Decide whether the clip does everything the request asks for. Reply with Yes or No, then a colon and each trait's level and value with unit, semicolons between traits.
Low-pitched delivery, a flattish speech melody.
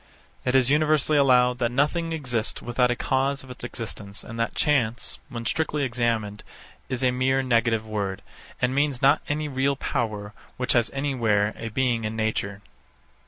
No: low, 125 Hz; average, 3.2 semitones